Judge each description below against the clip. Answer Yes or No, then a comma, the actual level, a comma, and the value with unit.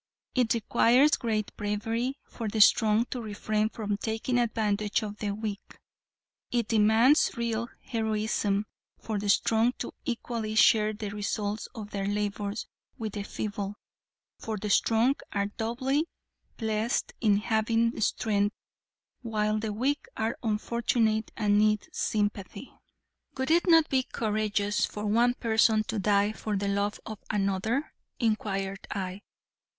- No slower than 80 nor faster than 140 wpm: Yes, slow, 135 wpm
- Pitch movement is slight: Yes, narrow, 1.9 semitones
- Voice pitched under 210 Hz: No, high, 215 Hz